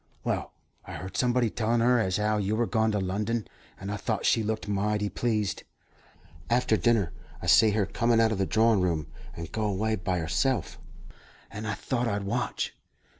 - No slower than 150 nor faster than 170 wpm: No, average, 185 wpm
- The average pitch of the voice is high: No, low, 105 Hz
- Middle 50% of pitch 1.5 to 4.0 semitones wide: Yes, narrow, 2.6 semitones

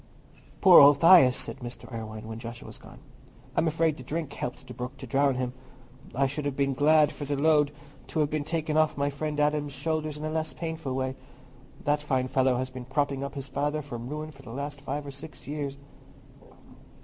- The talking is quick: Yes, fast, 210 wpm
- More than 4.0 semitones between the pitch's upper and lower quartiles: No, narrow, 2.5 semitones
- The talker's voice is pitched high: No, medium, 145 Hz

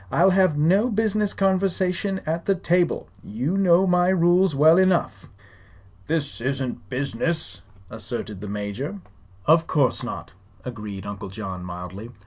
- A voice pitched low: No, medium, 160 Hz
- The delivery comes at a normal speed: No, slow, 130 wpm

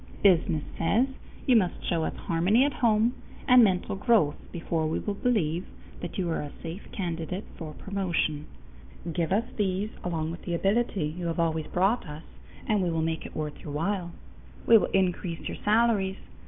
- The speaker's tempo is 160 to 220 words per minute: Yes, average, 180 wpm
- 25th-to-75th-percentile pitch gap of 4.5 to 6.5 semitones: No, average, 4.1 semitones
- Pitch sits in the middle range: Yes, medium, 180 Hz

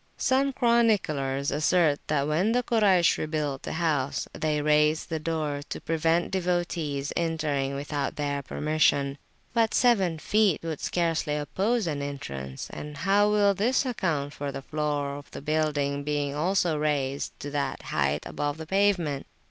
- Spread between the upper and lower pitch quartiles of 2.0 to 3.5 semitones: No, average, 4.0 semitones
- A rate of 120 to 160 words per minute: Yes, average, 150 wpm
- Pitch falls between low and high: Yes, medium, 155 Hz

